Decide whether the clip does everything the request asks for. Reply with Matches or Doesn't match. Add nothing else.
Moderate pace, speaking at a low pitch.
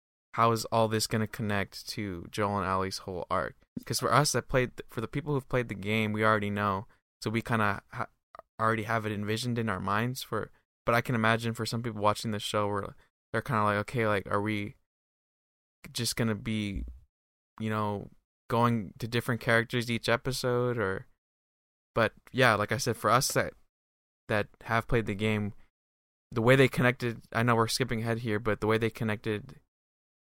Matches